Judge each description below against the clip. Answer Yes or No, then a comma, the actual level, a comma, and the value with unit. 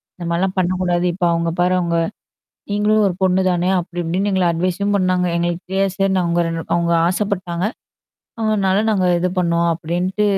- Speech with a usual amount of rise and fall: No, narrow, 1.9 semitones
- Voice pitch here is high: No, medium, 180 Hz